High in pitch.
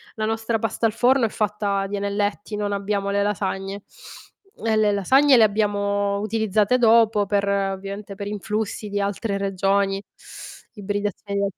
Yes: high, 205 Hz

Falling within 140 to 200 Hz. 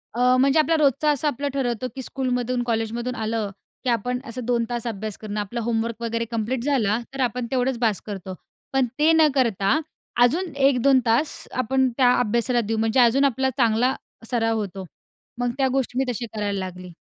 No: high, 240 Hz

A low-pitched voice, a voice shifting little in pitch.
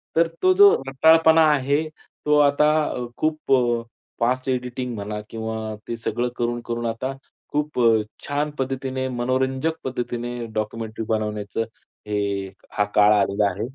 No: low, 125 Hz; average, 4.2 semitones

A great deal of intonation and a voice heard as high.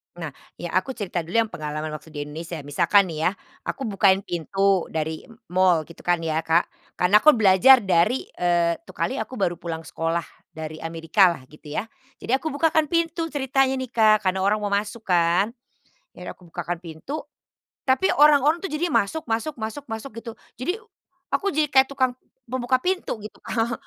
Yes: wide, 7.7 semitones; high, 200 Hz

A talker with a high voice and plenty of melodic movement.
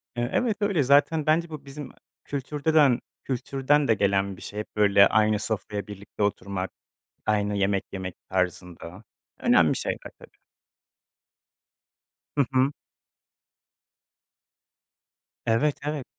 No: low, 115 Hz; wide, 6.5 semitones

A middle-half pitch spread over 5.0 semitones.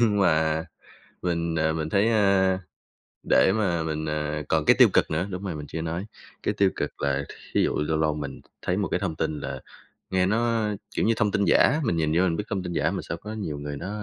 No: average, 4.2 semitones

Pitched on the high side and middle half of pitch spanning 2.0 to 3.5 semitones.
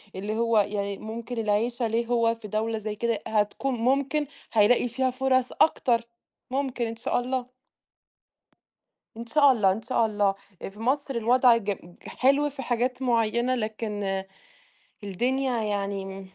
Yes: high, 230 Hz; average, 3.2 semitones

